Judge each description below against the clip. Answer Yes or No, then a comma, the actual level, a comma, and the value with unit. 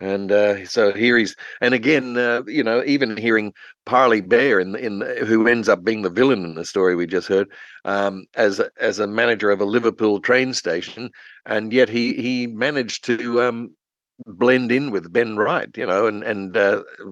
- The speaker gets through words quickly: No, average, 195 wpm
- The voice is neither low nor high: No, low, 115 Hz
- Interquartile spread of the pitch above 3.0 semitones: Yes, average, 3.4 semitones